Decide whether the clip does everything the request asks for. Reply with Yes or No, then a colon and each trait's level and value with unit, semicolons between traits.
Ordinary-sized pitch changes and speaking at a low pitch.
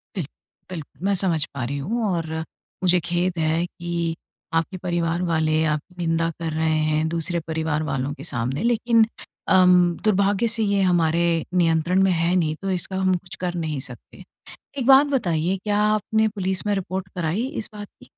No: average, 3.1 semitones; medium, 175 Hz